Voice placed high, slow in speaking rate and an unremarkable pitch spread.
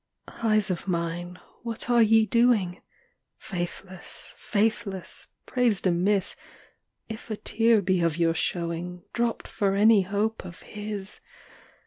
Yes: high, 200 Hz; slow, 125 wpm; average, 3.8 semitones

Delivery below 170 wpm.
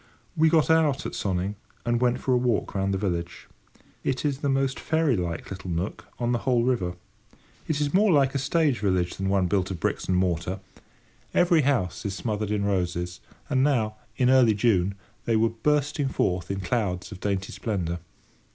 No: average, 190 wpm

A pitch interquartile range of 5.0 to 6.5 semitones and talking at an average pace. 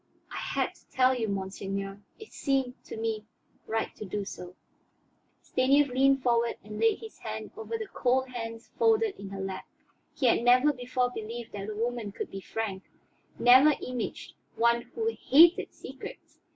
No: average, 3.9 semitones; average, 165 wpm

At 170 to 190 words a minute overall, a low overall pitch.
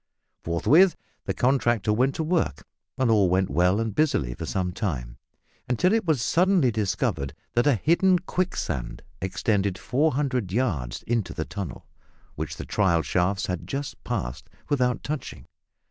No: average, 145 wpm; low, 110 Hz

